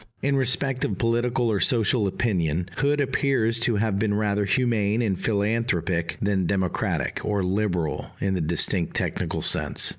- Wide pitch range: No, average, 3.9 semitones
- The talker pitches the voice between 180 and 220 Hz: No, low, 105 Hz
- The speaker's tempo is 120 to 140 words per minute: No, average, 150 wpm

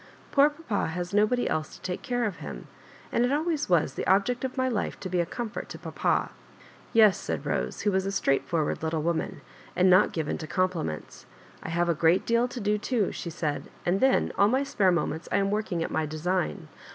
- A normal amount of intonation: No, wide, 5.9 semitones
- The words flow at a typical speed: No, fast, 225 wpm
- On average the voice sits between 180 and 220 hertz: Yes, high, 190 Hz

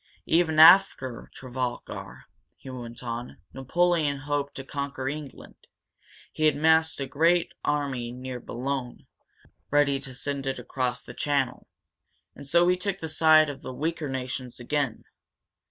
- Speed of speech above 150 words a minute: No, average, 140 wpm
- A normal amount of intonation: Yes, average, 3.3 semitones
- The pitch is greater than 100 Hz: Yes, medium, 140 Hz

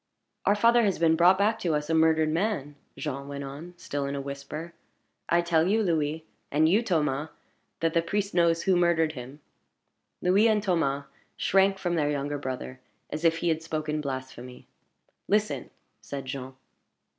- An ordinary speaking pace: Yes, average, 170 wpm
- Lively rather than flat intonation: No, average, 3.9 semitones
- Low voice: No, medium, 160 Hz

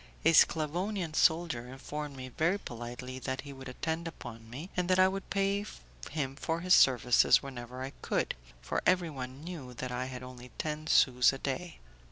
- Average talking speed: Yes, average, 180 wpm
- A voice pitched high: No, medium, 140 Hz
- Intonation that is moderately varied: Yes, average, 4.9 semitones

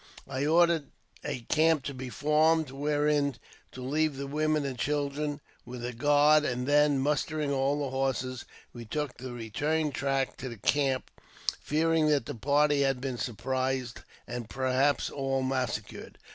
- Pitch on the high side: No, medium, 140 Hz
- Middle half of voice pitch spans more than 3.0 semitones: No, narrow, 2.5 semitones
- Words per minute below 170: Yes, average, 155 wpm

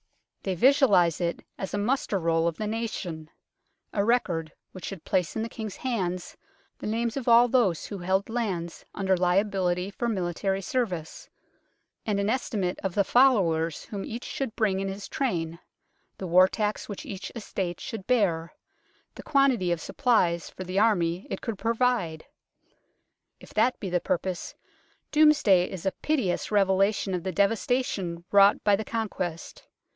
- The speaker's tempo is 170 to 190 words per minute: No, average, 160 wpm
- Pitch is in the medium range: No, high, 195 Hz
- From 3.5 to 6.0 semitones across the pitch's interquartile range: Yes, average, 4.2 semitones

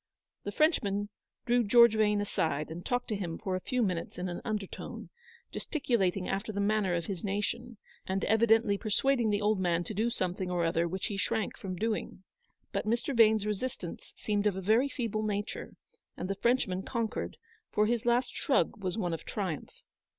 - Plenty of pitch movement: No, average, 3.5 semitones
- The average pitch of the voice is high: Yes, high, 210 Hz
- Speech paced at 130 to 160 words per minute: No, average, 185 wpm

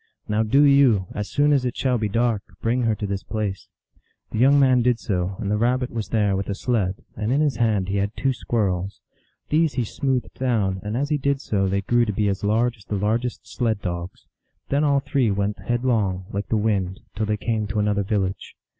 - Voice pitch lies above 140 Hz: No, low, 110 Hz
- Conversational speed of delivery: No, fast, 225 wpm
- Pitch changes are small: No, average, 3.8 semitones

